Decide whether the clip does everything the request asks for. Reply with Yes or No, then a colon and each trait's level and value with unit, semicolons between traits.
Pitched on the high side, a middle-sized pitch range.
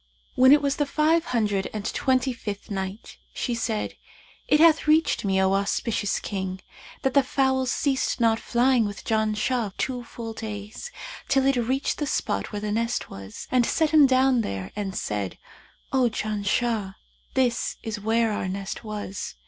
Yes: high, 230 Hz; average, 4.4 semitones